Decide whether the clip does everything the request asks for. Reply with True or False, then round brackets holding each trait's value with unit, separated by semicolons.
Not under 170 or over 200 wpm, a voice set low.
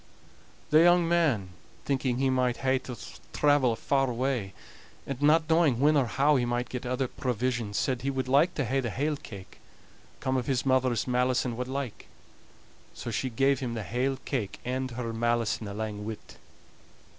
True (180 wpm; 130 Hz)